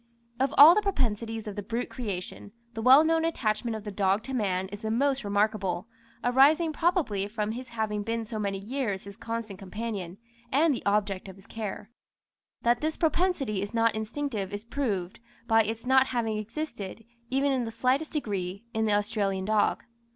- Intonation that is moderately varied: Yes, average, 4.2 semitones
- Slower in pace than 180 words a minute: No, average, 185 wpm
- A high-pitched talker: Yes, high, 225 Hz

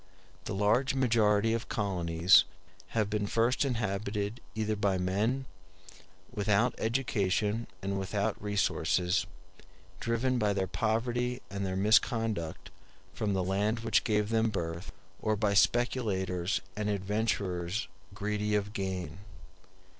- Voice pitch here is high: No, low, 105 Hz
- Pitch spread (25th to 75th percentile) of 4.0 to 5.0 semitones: No, average, 2.7 semitones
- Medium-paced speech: No, slow, 115 wpm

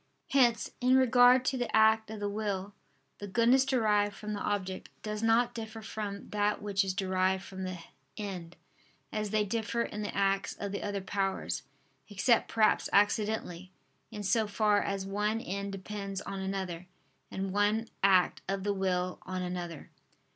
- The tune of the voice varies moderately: No, narrow, 2.3 semitones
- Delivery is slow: No, average, 165 wpm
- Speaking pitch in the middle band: No, high, 205 Hz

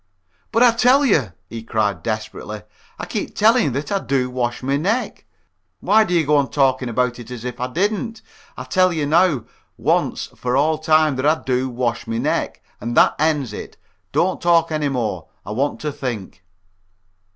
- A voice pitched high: No, medium, 140 Hz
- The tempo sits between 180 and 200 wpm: Yes, average, 190 wpm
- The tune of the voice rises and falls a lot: Yes, wide, 6.1 semitones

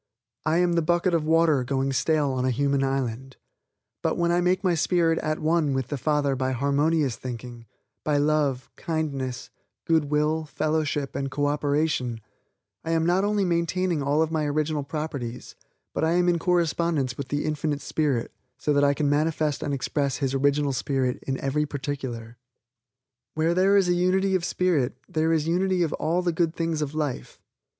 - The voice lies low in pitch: No, medium, 150 Hz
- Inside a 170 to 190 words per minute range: Yes, average, 180 wpm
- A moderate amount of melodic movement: Yes, average, 3.3 semitones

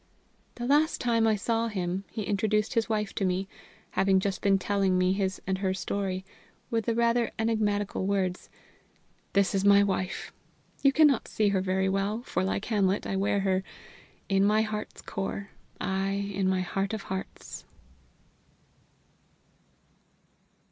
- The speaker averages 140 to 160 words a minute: Yes, average, 150 wpm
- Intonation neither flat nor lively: No, narrow, 2.3 semitones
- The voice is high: Yes, high, 200 Hz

